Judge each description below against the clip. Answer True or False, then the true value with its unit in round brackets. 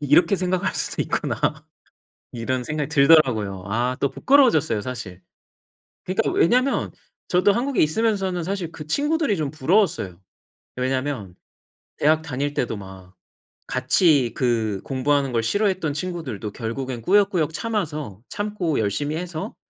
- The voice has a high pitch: False (150 Hz)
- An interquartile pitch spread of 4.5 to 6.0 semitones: False (7.0 semitones)